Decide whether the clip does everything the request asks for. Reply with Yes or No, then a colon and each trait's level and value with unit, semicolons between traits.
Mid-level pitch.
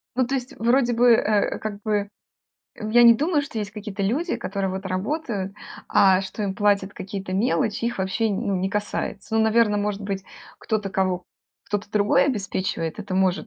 No: high, 205 Hz